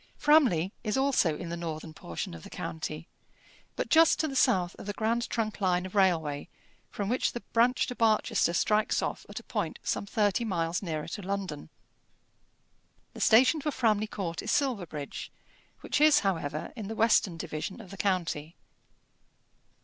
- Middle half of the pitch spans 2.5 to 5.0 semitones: No, wide, 5.6 semitones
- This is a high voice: Yes, high, 200 Hz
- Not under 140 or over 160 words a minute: No, average, 170 wpm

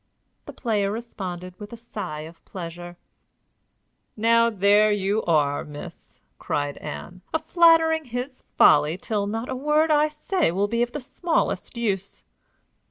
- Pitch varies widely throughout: Yes, wide, 5.9 semitones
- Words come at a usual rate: Yes, average, 150 wpm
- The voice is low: No, high, 215 Hz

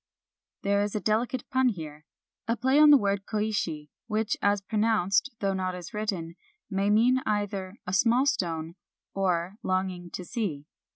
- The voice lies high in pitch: Yes, high, 200 Hz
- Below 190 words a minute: Yes, average, 175 wpm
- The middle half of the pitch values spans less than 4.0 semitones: Yes, average, 3.3 semitones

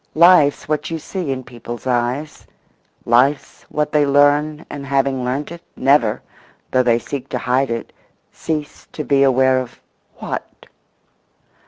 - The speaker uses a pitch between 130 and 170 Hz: Yes, medium, 140 Hz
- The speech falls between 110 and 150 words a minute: Yes, average, 140 wpm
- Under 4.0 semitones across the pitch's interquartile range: Yes, average, 2.8 semitones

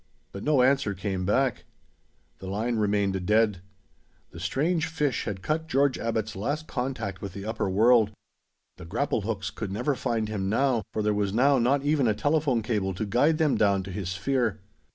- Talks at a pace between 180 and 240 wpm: Yes, average, 185 wpm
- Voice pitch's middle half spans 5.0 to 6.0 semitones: Yes, average, 5.3 semitones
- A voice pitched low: Yes, low, 110 Hz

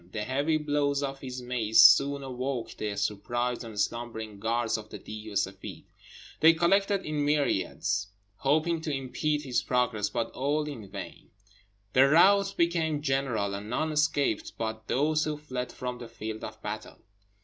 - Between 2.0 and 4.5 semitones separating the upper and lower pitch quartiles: No, average, 5.2 semitones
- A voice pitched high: No, low, 130 Hz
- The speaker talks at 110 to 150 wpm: No, average, 160 wpm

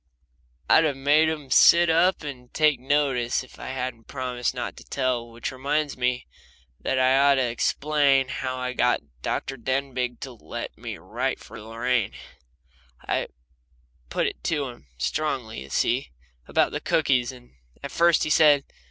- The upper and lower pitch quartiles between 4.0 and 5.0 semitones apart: No, average, 2.9 semitones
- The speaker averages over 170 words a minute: No, average, 165 wpm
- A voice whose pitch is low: Yes, low, 130 Hz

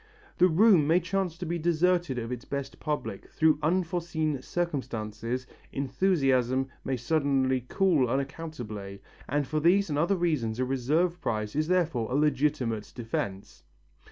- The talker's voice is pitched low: No, medium, 145 Hz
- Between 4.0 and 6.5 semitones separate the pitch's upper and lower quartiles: Yes, average, 5.2 semitones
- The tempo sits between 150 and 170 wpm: No, average, 140 wpm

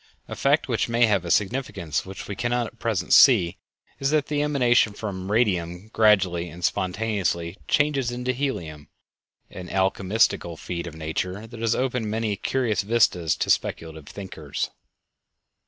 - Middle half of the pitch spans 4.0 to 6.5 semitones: Yes, average, 5.3 semitones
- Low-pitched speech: Yes, low, 105 Hz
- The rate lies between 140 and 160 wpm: Yes, average, 150 wpm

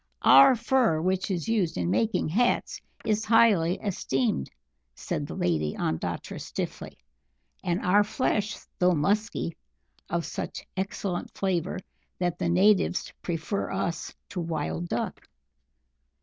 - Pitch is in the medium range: Yes, medium, 180 Hz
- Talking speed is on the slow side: Yes, slow, 120 wpm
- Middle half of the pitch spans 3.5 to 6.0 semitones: Yes, average, 4.3 semitones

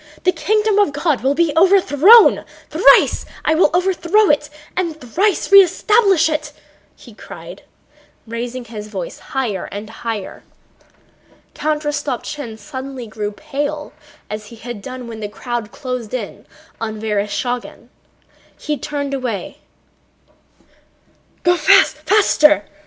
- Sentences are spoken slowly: Yes, slow, 115 wpm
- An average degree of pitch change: No, wide, 5.9 semitones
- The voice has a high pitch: Yes, very high, 275 Hz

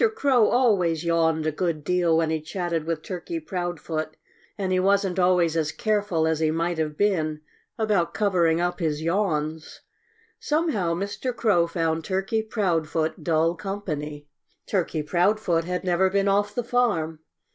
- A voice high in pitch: No, medium, 175 Hz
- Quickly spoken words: No, average, 150 wpm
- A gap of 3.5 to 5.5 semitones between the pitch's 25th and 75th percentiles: Yes, average, 3.8 semitones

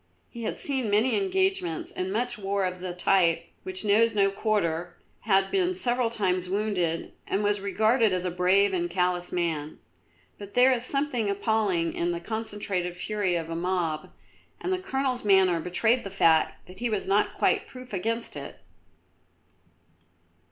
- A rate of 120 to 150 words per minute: No, average, 165 wpm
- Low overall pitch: No, high, 200 Hz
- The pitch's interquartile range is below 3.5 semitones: No, average, 4.3 semitones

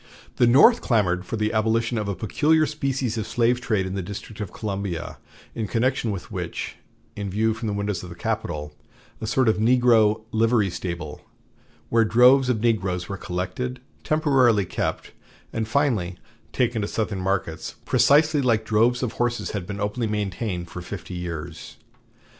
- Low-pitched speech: Yes, low, 110 Hz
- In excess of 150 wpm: Yes, average, 165 wpm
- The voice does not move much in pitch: No, average, 4.0 semitones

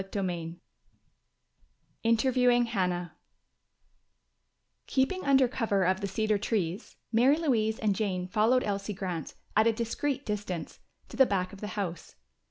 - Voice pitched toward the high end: Yes, high, 210 Hz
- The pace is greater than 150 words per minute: No, slow, 135 wpm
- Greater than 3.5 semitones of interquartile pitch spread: Yes, average, 4.4 semitones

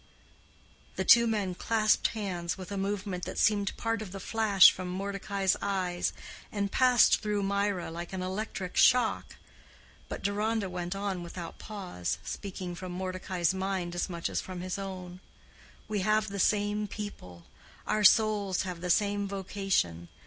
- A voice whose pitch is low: No, high, 195 Hz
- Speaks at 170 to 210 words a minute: No, average, 155 wpm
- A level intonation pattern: Yes, narrow, 2.3 semitones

